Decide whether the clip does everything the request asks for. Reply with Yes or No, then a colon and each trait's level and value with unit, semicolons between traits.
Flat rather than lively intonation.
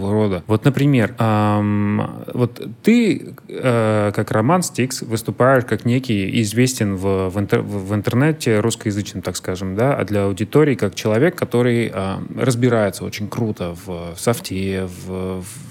No: average, 3.7 semitones